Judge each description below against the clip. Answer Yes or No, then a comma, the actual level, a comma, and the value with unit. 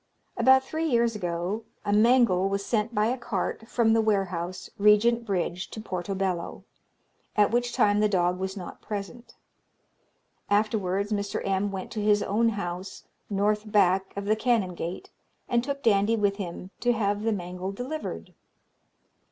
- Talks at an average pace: Yes, average, 150 wpm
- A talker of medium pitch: No, high, 205 Hz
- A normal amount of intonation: Yes, average, 3.0 semitones